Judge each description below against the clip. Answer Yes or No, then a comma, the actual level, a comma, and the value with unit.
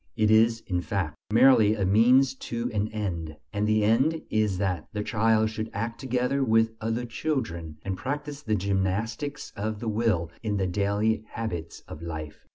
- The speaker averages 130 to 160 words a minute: No, average, 170 wpm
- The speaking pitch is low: Yes, low, 110 Hz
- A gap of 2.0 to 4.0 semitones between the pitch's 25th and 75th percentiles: Yes, average, 3.0 semitones